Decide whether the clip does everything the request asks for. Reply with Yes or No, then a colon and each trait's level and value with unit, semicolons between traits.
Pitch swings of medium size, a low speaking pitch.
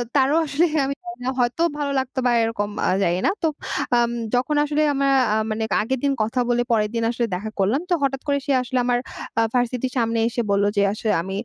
No: average, 3.6 semitones; high, 245 Hz